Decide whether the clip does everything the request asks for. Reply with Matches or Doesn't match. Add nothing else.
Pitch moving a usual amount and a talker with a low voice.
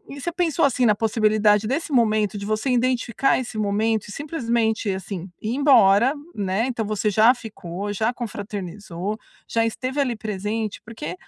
Doesn't match